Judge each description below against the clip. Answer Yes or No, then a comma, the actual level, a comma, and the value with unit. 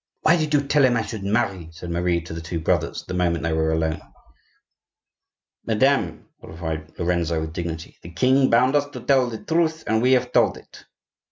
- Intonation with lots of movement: Yes, wide, 7.9 semitones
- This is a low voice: Yes, very low, 90 Hz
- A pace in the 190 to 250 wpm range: Yes, average, 195 wpm